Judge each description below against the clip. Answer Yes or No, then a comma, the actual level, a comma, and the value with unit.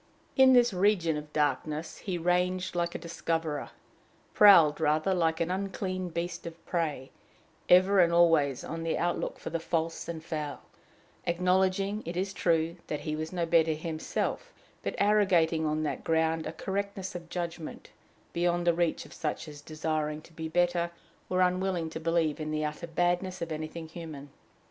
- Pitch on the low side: No, medium, 170 Hz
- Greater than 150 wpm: Yes, average, 170 wpm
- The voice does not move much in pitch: Yes, narrow, 2.3 semitones